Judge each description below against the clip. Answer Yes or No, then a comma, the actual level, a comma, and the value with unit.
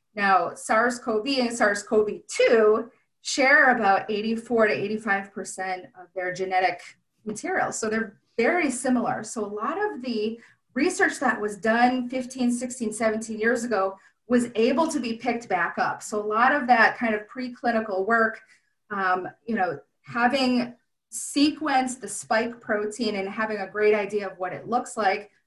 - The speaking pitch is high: Yes, high, 225 Hz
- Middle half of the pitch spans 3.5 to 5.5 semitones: No, average, 3.1 semitones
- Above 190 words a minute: No, average, 155 wpm